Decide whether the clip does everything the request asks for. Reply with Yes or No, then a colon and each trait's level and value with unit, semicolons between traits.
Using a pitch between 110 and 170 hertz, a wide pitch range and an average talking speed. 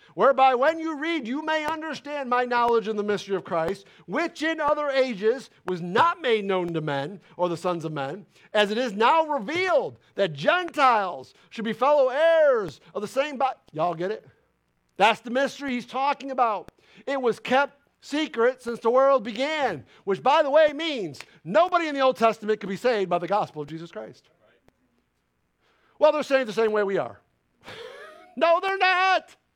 No: very high, 260 Hz; wide, 6.5 semitones; average, 185 wpm